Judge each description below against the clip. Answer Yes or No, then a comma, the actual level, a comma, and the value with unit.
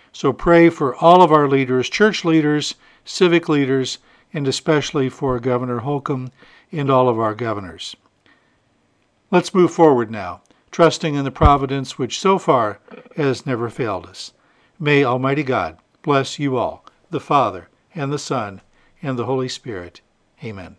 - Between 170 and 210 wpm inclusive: No, average, 150 wpm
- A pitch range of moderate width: Yes, average, 3.9 semitones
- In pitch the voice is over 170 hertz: No, medium, 140 Hz